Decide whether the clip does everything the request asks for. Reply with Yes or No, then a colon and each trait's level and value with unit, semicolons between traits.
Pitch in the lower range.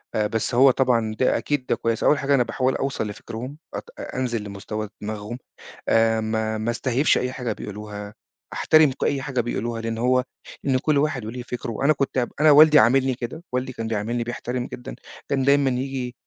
Yes: low, 125 Hz